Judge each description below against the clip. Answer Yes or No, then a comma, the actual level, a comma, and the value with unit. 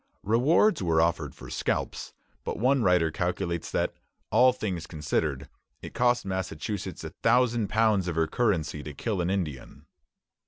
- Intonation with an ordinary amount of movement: No, wide, 5.7 semitones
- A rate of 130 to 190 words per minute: Yes, average, 150 wpm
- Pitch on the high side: No, very low, 95 Hz